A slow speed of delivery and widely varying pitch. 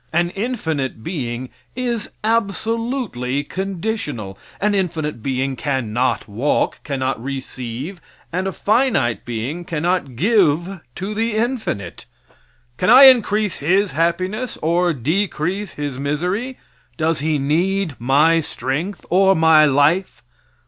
Yes: slow, 115 wpm; wide, 6.4 semitones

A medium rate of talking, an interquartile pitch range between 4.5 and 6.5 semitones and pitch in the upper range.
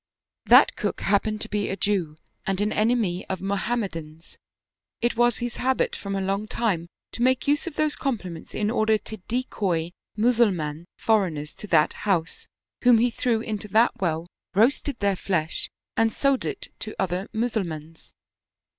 Yes: average, 160 wpm; average, 4.8 semitones; high, 210 Hz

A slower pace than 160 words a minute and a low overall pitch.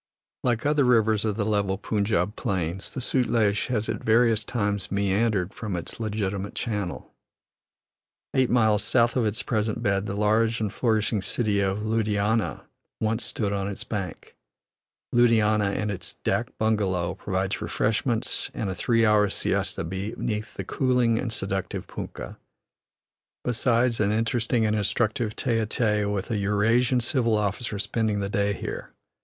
Yes: average, 150 wpm; low, 110 Hz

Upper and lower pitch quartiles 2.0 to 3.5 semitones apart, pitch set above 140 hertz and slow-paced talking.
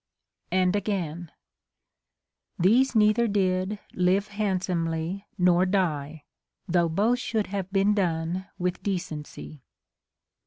Yes: average, 2.9 semitones; medium, 185 Hz; slow, 105 wpm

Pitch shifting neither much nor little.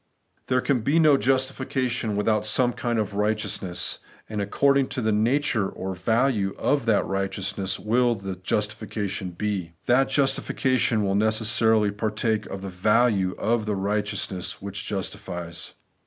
Yes: average, 3.6 semitones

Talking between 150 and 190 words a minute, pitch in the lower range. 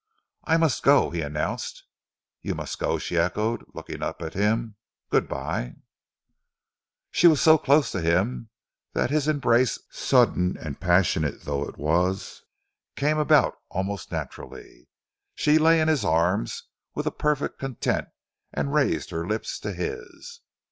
No: average, 140 wpm; low, 105 Hz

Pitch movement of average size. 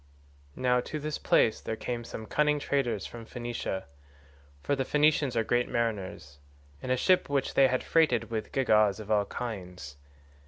Yes: average, 4.1 semitones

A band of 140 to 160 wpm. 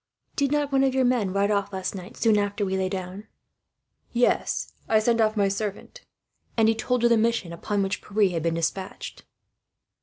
No: average, 195 wpm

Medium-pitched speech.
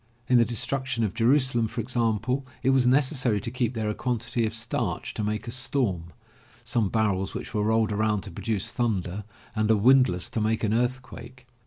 No: low, 115 Hz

